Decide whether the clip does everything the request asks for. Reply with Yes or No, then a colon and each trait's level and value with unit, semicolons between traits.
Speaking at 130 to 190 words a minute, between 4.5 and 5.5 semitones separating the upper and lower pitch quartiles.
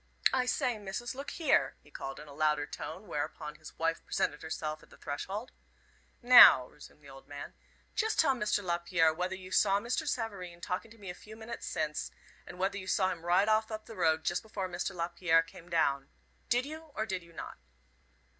No: average, 200 wpm; average, 5.2 semitones